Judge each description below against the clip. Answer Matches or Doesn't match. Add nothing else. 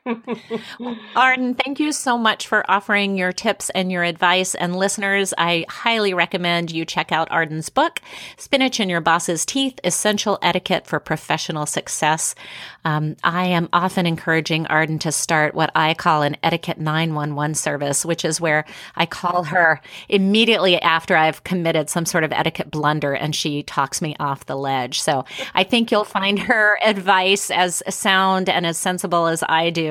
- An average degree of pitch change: Matches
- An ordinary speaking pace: Matches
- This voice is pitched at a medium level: Matches